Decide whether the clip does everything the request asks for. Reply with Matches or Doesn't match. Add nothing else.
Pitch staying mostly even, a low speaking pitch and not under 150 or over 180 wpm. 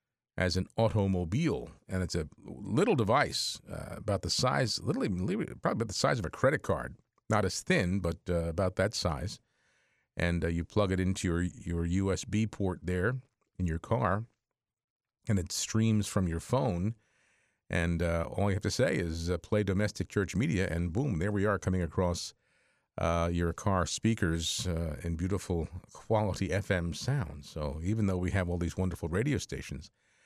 Doesn't match